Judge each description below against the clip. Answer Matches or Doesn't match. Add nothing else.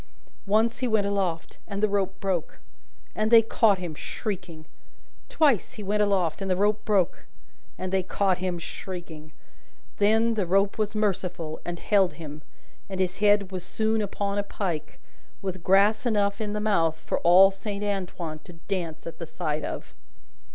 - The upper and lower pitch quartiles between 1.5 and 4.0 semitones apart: Matches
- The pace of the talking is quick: Doesn't match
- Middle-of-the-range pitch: Doesn't match